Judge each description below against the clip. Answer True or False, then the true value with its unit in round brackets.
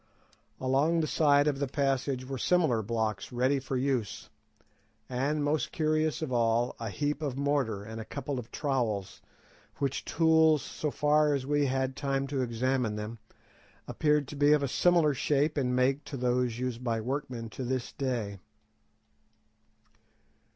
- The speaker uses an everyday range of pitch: True (3.1 semitones)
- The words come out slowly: False (160 wpm)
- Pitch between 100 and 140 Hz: True (135 Hz)